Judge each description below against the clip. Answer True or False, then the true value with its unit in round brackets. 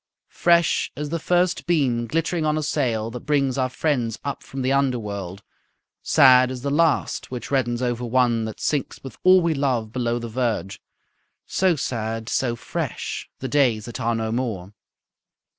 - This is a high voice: False (125 Hz)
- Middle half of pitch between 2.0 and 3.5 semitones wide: False (3.9 semitones)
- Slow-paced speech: False (170 wpm)